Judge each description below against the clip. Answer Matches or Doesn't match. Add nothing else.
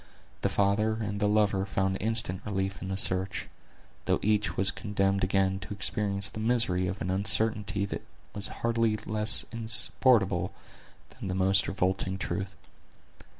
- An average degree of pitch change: Doesn't match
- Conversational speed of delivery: Matches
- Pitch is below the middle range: Matches